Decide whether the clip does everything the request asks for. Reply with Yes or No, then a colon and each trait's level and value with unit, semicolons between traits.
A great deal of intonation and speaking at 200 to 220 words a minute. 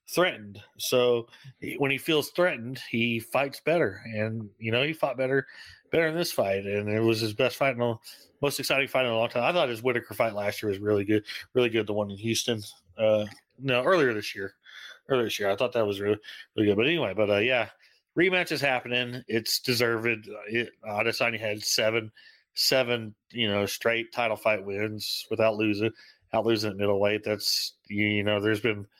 No: average, 2.9 semitones; fast, 205 wpm